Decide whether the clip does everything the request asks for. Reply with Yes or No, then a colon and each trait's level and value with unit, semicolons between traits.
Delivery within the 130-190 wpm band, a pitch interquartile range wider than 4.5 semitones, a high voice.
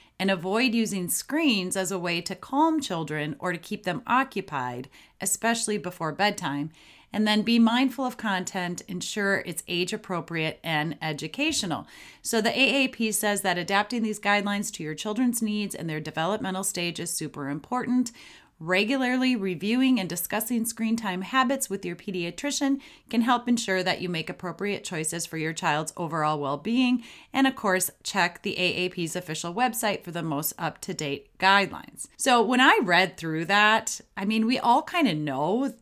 Yes: average, 170 wpm; wide, 5.5 semitones; high, 195 Hz